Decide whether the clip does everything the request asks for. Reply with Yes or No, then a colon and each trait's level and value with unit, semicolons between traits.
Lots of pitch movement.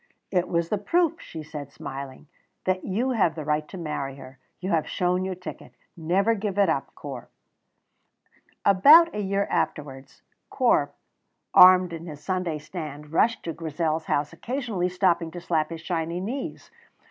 No: average, 3.9 semitones